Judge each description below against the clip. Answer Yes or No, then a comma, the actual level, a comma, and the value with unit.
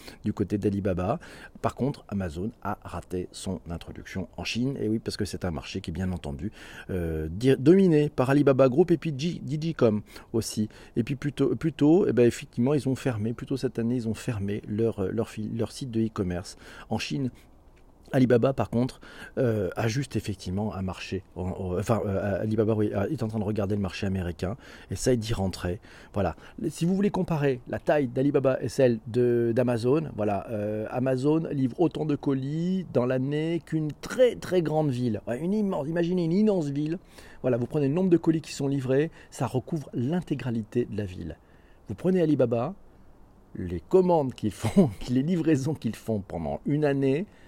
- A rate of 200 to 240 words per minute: No, average, 185 wpm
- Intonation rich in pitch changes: Yes, wide, 6.0 semitones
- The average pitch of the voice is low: Yes, low, 120 Hz